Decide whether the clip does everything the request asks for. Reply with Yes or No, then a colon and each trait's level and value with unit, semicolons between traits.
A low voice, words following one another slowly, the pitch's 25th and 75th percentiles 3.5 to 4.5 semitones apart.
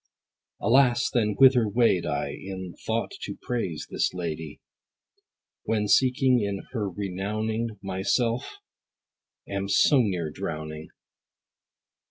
Yes: low, 105 Hz; slow, 105 wpm; average, 4.2 semitones